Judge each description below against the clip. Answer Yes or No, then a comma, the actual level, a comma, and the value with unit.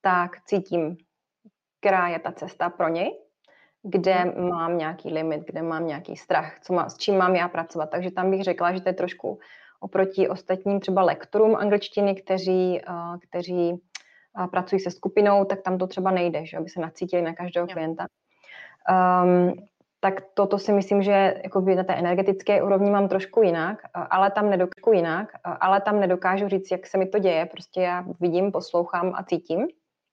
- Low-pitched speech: No, medium, 185 Hz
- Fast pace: Yes, fast, 175 wpm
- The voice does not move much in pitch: Yes, narrow, 1.9 semitones